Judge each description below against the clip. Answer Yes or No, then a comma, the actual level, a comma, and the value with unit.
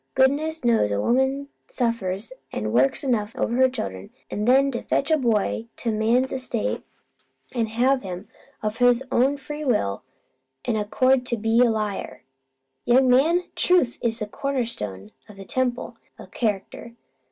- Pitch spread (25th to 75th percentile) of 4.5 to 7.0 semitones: No, average, 3.9 semitones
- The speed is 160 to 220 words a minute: No, average, 150 wpm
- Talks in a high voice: Yes, high, 235 Hz